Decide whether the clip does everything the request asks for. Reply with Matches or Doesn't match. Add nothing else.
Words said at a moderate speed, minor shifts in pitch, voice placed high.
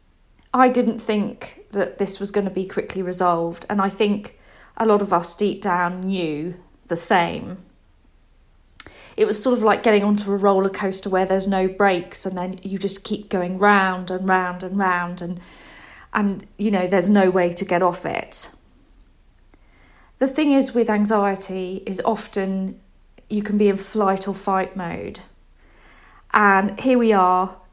Matches